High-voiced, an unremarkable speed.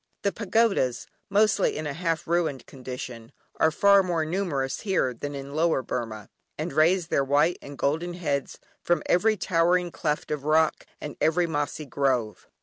No: medium, 155 Hz; average, 160 wpm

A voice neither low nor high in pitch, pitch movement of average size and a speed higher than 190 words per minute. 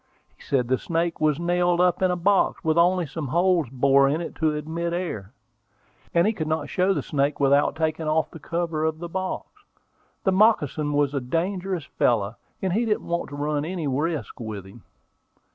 Yes: medium, 160 Hz; average, 3.6 semitones; average, 200 wpm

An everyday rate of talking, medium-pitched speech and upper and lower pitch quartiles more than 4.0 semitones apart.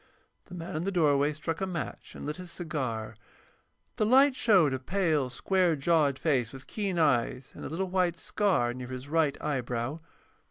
Yes: average, 185 wpm; medium, 155 Hz; wide, 5.5 semitones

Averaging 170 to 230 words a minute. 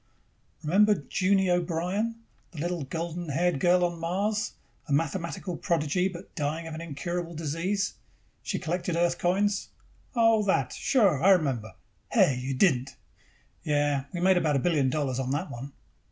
No: average, 155 wpm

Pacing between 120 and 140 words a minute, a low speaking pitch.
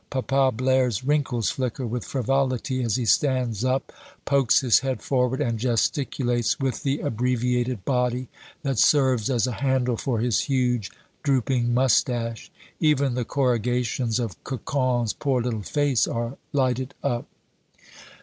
Yes: slow, 135 wpm; low, 125 Hz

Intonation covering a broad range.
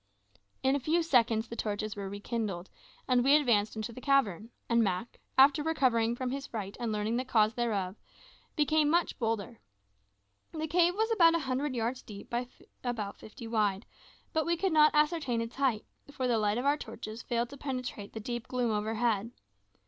No: average, 4.5 semitones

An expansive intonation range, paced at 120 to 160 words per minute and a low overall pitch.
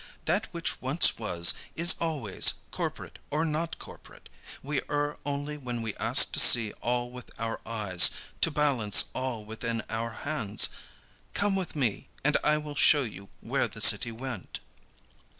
No: average, 4.9 semitones; average, 155 wpm; low, 125 Hz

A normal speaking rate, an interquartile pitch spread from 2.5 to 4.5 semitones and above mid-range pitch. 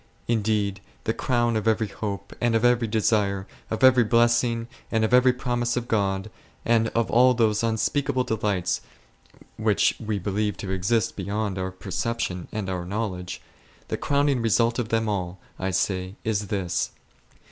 No: average, 160 wpm; average, 3.0 semitones; low, 110 Hz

